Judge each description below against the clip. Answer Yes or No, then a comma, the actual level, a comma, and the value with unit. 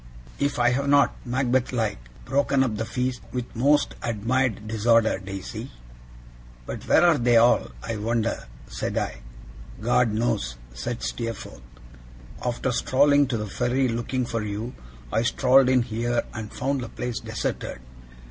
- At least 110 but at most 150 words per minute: Yes, average, 145 wpm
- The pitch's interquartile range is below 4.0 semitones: Yes, narrow, 2.6 semitones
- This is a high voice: No, low, 120 Hz